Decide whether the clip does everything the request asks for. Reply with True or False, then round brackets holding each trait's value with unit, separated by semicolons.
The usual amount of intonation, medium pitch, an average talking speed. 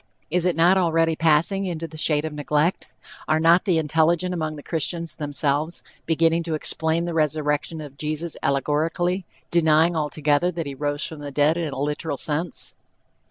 False (2.1 semitones; 160 Hz; 170 wpm)